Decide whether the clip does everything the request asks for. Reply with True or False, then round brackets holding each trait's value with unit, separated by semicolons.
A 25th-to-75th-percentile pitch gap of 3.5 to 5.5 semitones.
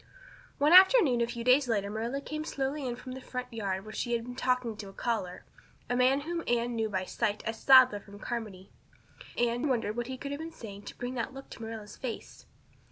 False (3.1 semitones)